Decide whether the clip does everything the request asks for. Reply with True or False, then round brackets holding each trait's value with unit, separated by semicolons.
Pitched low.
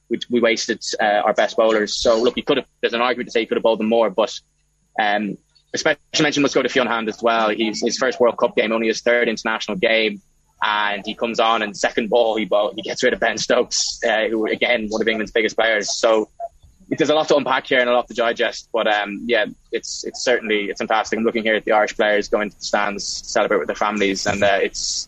True (110 Hz)